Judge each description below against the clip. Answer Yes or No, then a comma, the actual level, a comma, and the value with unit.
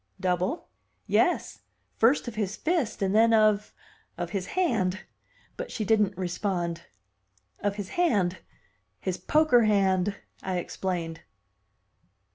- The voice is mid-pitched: No, high, 200 Hz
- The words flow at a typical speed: No, slow, 115 wpm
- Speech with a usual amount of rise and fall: Yes, average, 3.5 semitones